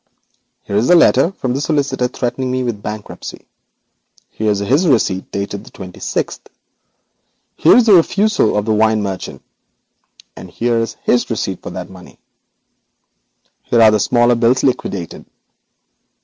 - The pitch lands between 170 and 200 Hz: No, low, 115 Hz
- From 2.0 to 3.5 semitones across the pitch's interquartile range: No, average, 4.2 semitones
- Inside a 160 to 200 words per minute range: No, average, 150 wpm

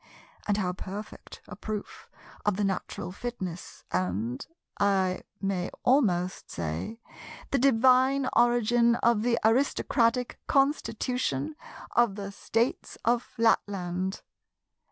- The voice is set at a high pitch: Yes, high, 210 Hz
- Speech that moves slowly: Yes, slow, 105 wpm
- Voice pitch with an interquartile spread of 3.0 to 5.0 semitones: Yes, average, 4.6 semitones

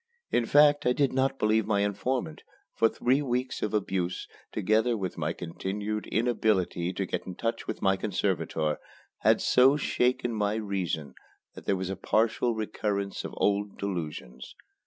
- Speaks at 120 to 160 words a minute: Yes, average, 155 wpm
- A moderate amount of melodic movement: Yes, average, 4.2 semitones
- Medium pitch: No, low, 105 Hz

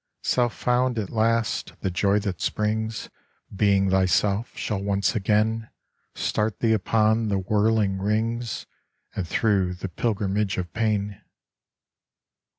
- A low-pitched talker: Yes, low, 105 Hz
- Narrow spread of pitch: Yes, narrow, 2.3 semitones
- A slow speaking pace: Yes, slow, 120 wpm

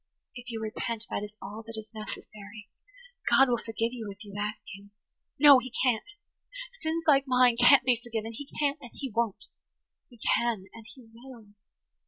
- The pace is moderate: Yes, average, 175 wpm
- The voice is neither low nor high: No, high, 230 Hz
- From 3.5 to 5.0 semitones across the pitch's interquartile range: No, average, 2.9 semitones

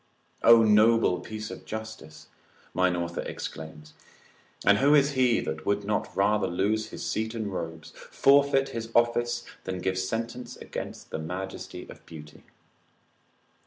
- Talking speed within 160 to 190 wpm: No, average, 140 wpm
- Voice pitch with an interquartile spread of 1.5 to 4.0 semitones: No, average, 4.5 semitones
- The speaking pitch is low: Yes, low, 105 Hz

